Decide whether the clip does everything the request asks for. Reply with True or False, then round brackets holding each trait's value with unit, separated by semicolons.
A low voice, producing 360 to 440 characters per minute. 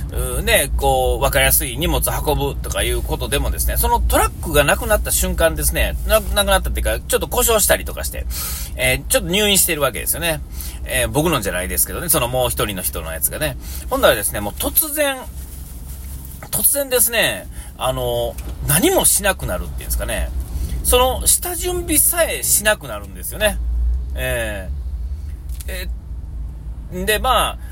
True (75 Hz; 365 characters per minute)